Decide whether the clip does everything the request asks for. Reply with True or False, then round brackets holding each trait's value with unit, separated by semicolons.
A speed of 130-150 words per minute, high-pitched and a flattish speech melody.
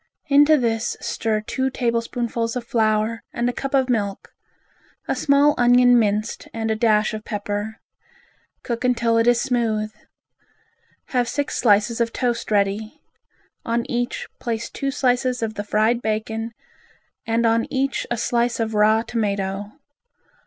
True (145 wpm; 230 Hz; 2.2 semitones)